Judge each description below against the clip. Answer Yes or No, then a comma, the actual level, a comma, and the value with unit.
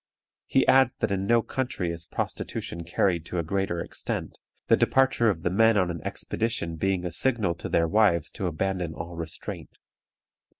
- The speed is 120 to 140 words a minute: No, average, 175 wpm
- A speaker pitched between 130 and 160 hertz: No, very low, 90 Hz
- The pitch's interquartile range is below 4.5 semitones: No, average, 4.8 semitones